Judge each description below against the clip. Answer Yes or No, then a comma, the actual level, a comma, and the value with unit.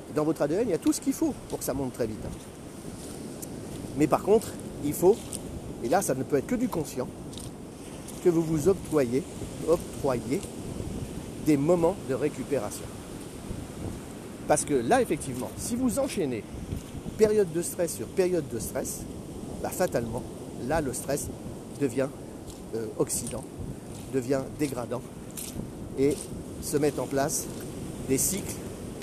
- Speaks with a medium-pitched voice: Yes, medium, 145 Hz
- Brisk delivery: No, slow, 145 wpm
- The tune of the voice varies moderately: No, wide, 6.1 semitones